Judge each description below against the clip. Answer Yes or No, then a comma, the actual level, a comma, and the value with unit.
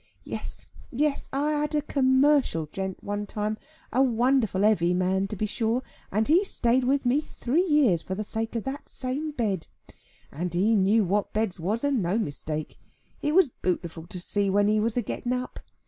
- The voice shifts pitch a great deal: Yes, wide, 5.7 semitones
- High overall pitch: Yes, high, 220 Hz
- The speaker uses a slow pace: No, average, 190 wpm